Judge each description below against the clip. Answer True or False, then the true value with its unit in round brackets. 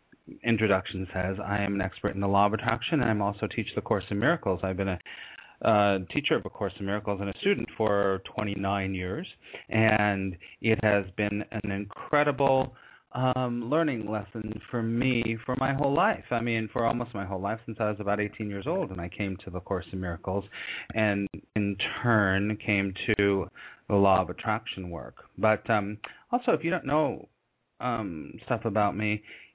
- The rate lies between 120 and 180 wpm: False (190 wpm)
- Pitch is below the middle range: True (105 Hz)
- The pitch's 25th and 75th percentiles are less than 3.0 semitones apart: True (2.6 semitones)